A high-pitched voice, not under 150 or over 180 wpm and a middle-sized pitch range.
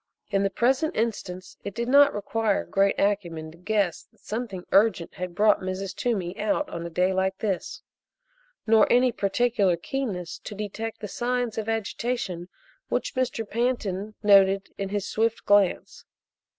Yes: high, 205 Hz; average, 155 wpm; average, 3.3 semitones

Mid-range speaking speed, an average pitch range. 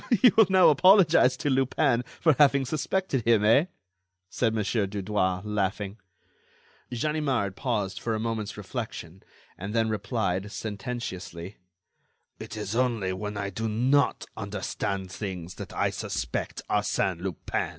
No: slow, 130 wpm; average, 4.8 semitones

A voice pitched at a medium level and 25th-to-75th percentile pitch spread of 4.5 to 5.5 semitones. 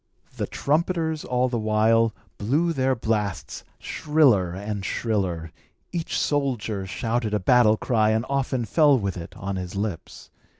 No: low, 115 Hz; average, 4.8 semitones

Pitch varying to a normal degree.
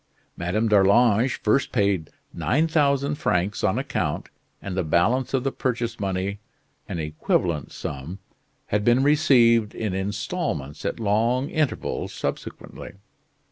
No: wide, 5.8 semitones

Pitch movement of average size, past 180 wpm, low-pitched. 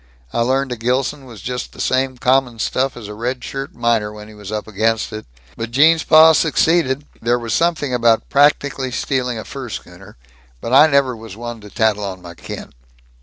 Yes: average, 3.7 semitones; average, 200 wpm; low, 120 Hz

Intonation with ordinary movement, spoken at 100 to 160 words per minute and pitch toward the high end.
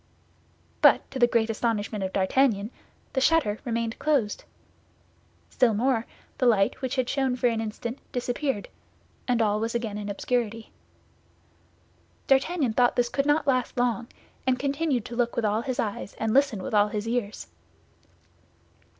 Yes: average, 3.2 semitones; average, 155 wpm; high, 235 Hz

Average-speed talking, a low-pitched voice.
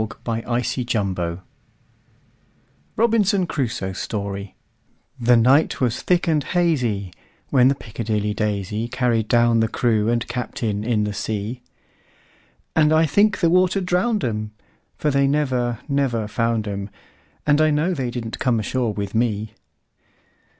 No: slow, 115 wpm; low, 120 Hz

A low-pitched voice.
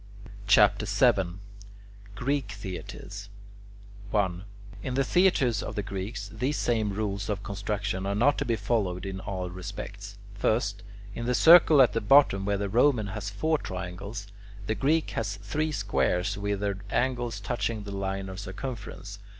Yes: low, 105 Hz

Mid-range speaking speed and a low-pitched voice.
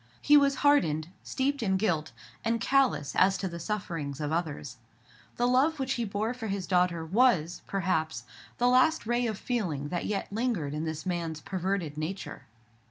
No: average, 170 wpm; high, 190 Hz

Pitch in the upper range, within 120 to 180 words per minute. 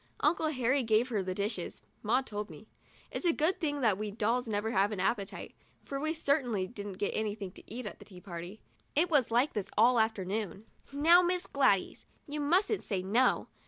No: high, 225 Hz; average, 195 wpm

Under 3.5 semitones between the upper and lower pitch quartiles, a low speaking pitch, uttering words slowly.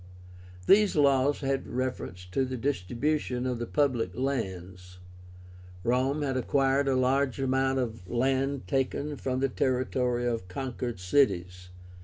Yes: narrow, 2.5 semitones; low, 130 Hz; slow, 130 wpm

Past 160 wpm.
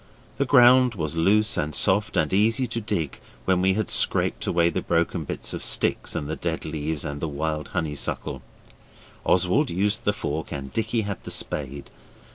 Yes: average, 180 wpm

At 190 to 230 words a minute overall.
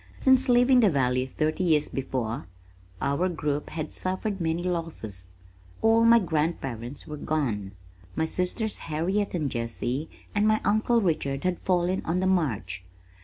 No: average, 145 wpm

